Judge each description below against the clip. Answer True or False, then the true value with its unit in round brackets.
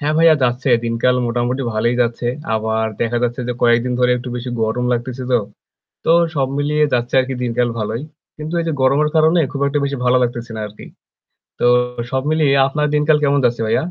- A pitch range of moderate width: True (3.3 semitones)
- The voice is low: True (125 Hz)